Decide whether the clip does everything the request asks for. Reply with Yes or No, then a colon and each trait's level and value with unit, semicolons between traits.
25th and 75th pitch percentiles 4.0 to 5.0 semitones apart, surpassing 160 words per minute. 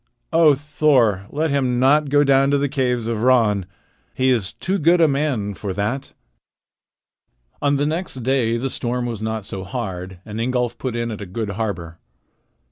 Yes: average, 4.7 semitones; average, 180 wpm